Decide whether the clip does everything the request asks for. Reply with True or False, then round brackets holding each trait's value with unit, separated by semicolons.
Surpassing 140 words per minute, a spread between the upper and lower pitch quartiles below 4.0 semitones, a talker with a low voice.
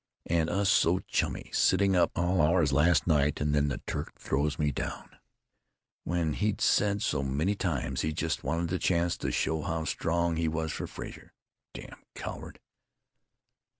True (165 wpm; 2.8 semitones; 80 Hz)